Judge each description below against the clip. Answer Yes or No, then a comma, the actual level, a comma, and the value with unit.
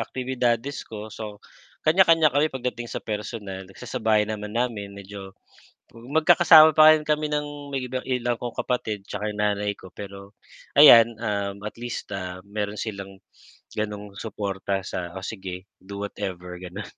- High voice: No, low, 105 Hz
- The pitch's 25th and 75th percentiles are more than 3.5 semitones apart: Yes, average, 3.9 semitones